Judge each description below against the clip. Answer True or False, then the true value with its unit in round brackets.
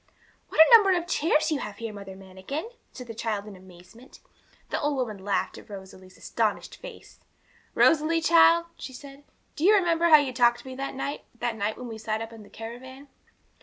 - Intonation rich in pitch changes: True (6.5 semitones)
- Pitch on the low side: False (250 Hz)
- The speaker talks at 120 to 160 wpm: False (205 wpm)